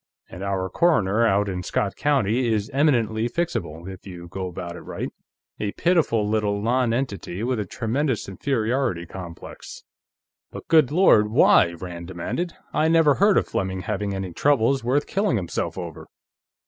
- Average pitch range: No, wide, 6.3 semitones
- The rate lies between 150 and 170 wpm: Yes, average, 155 wpm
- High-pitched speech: No, low, 110 Hz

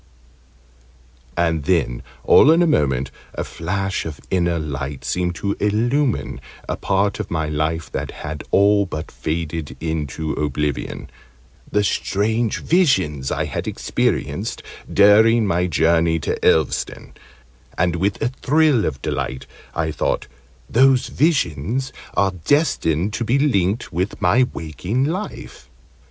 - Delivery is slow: Yes, slow, 130 wpm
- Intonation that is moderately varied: No, wide, 6.3 semitones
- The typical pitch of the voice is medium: No, very low, 90 Hz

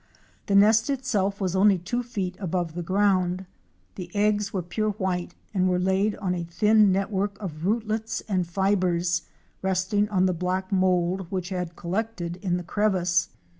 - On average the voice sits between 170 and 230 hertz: Yes, high, 190 Hz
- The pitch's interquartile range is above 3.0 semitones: No, narrow, 2.4 semitones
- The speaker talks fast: No, average, 165 wpm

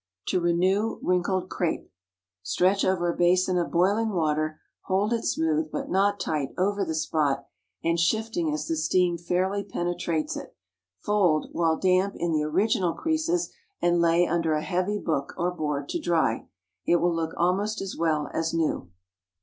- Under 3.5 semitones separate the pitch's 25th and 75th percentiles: Yes, average, 2.9 semitones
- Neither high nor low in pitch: Yes, medium, 175 Hz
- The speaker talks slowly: No, average, 165 wpm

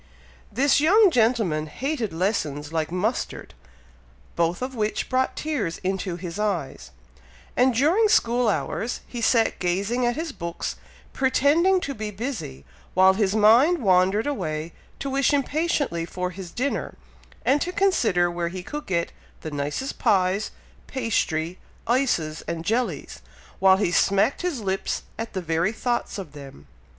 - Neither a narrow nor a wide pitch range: No, wide, 7.1 semitones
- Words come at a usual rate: Yes, average, 145 wpm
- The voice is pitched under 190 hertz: No, high, 210 Hz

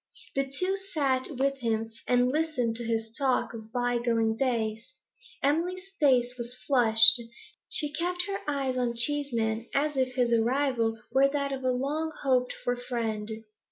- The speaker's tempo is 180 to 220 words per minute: No, average, 155 wpm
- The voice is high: Yes, very high, 255 Hz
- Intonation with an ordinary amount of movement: Yes, average, 3.2 semitones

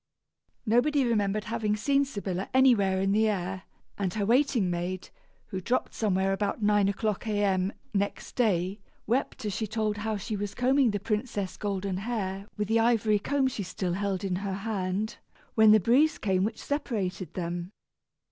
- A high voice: Yes, high, 205 Hz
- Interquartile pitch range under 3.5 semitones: Yes, average, 2.8 semitones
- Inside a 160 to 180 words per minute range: Yes, average, 165 wpm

